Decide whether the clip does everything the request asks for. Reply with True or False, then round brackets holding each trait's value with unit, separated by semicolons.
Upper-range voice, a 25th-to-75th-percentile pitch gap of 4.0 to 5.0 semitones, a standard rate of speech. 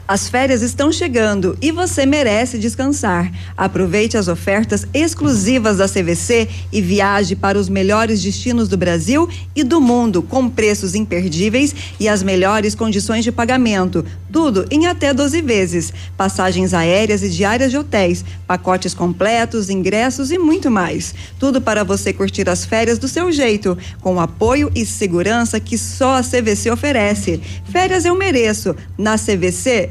False (210 Hz; 5.4 semitones; 150 wpm)